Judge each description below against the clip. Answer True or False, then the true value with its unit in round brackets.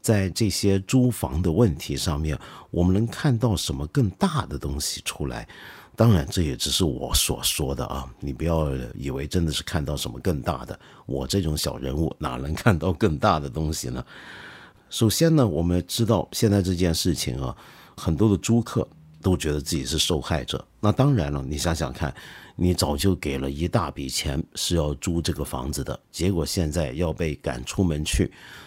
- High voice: False (85 Hz)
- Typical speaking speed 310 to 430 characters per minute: False (270 characters per minute)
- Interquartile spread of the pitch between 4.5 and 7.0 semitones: True (5.3 semitones)